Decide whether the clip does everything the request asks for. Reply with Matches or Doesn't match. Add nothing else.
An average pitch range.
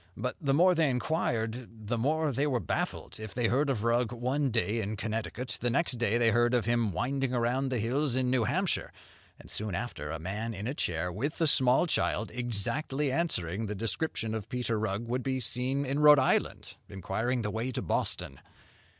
Matches